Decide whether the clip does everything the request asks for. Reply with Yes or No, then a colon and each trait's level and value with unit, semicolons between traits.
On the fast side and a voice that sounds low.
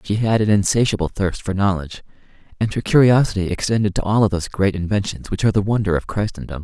Yes: fast, 210 wpm; low, 100 Hz